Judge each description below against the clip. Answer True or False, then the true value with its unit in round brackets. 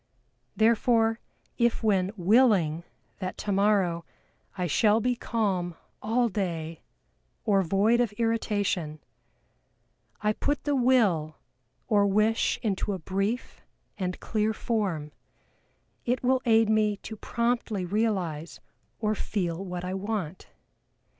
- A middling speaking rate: False (115 wpm)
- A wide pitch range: False (3.6 semitones)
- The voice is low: False (210 Hz)